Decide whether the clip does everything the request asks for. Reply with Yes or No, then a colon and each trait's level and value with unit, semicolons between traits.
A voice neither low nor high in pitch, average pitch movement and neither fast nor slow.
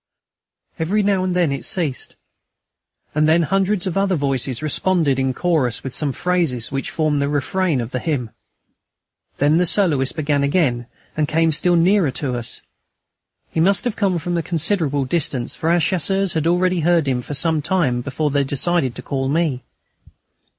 Yes: medium, 155 Hz; average, 4.5 semitones; average, 170 wpm